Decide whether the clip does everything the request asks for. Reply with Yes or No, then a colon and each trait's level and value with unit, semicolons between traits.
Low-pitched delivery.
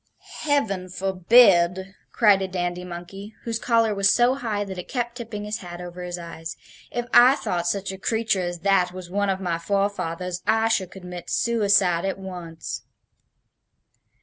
No: high, 190 Hz